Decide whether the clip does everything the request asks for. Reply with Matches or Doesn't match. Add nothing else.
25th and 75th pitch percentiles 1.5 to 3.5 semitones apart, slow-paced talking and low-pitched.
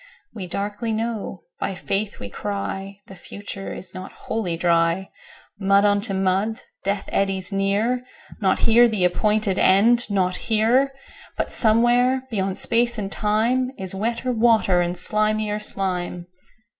Doesn't match